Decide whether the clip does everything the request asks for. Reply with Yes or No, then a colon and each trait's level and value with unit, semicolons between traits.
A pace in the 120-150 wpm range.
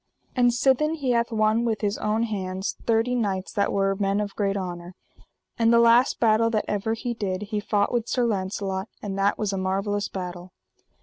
No: average, 195 wpm